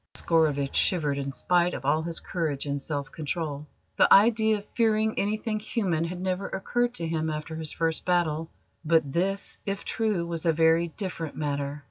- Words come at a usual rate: Yes, average, 175 wpm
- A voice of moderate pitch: Yes, medium, 165 Hz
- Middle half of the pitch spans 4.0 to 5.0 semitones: Yes, average, 4.3 semitones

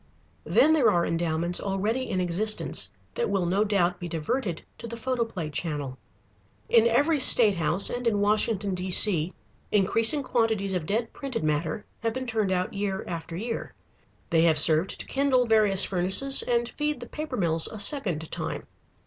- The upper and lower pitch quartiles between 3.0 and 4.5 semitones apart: No, average, 5.2 semitones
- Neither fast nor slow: Yes, average, 165 wpm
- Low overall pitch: No, high, 200 Hz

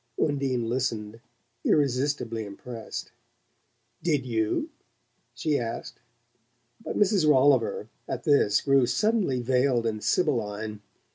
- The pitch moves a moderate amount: Yes, average, 4.1 semitones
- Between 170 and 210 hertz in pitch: No, low, 125 Hz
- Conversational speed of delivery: No, slow, 95 wpm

